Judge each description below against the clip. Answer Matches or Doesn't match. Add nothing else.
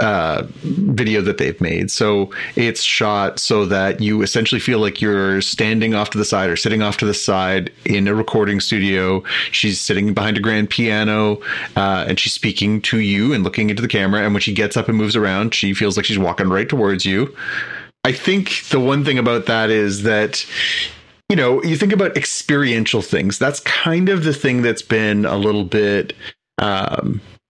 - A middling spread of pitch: Doesn't match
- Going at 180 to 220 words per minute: Matches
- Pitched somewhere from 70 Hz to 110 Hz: Matches